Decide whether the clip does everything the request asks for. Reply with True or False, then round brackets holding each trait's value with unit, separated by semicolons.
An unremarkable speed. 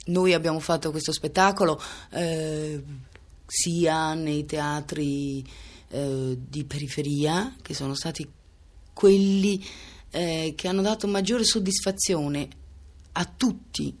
False (105 wpm)